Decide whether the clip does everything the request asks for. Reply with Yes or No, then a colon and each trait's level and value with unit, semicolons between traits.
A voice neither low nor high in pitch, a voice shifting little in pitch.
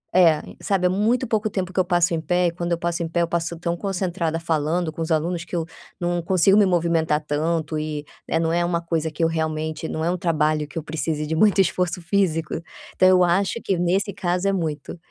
Yes: medium, 170 Hz; narrow, 2.1 semitones